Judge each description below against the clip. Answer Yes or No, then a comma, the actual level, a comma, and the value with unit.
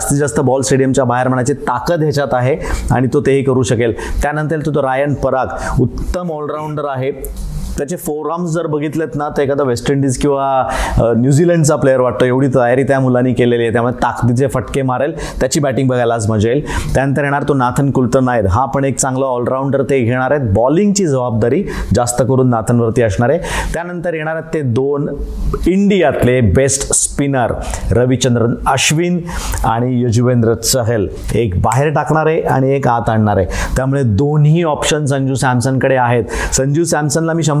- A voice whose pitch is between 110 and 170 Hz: Yes, low, 135 Hz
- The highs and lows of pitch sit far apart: No, average, 3.1 semitones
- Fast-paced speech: Yes, fast, 170 wpm